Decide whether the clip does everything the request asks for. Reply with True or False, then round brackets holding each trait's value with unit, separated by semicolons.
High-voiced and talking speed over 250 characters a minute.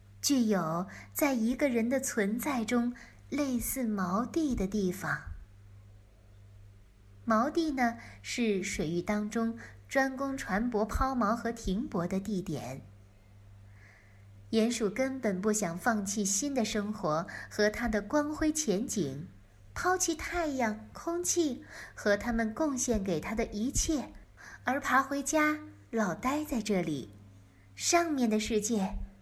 False (215 Hz; 175 characters per minute)